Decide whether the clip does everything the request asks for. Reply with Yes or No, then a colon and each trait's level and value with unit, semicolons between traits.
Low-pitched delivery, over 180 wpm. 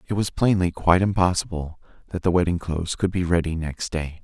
Yes: very low, 85 Hz; average, 200 wpm